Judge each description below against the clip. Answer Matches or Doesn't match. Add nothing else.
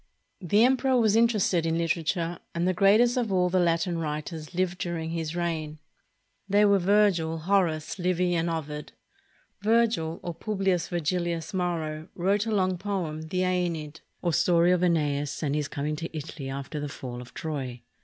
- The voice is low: Doesn't match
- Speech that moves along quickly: Doesn't match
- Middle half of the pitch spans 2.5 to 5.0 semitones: Matches